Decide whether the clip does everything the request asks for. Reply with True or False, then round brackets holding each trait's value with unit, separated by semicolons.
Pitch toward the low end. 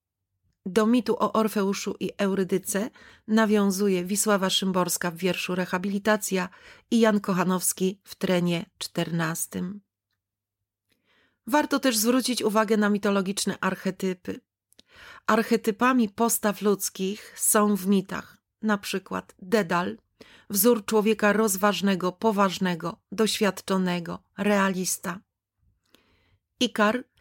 False (200 Hz)